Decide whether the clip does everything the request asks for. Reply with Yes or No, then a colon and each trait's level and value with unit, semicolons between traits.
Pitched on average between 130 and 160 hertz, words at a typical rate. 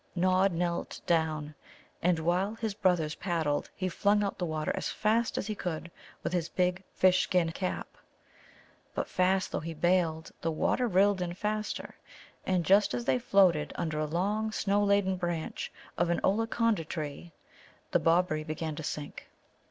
No: medium, 180 Hz; average, 165 wpm